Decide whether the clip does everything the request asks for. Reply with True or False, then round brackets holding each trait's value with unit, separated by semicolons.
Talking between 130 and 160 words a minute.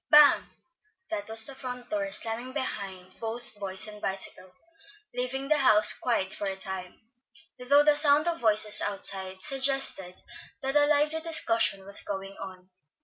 True (150 wpm)